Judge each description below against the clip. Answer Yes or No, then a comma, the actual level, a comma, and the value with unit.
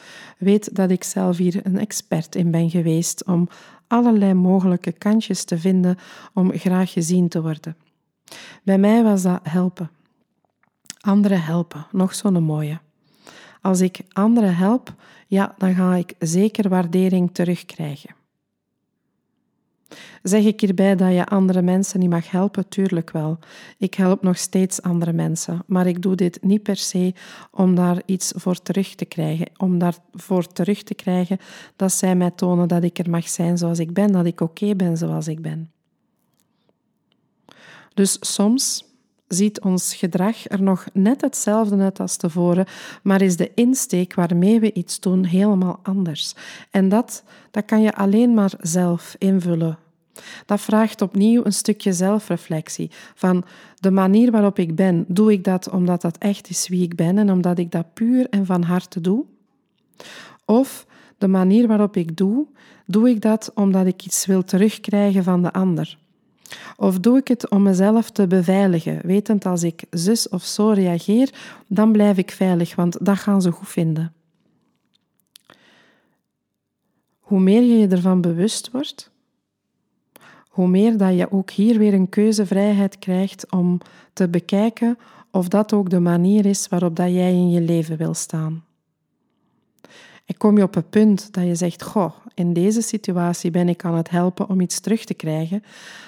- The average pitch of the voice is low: No, high, 190 Hz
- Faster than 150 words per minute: Yes, average, 160 wpm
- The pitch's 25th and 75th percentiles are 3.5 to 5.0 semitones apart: No, average, 2.7 semitones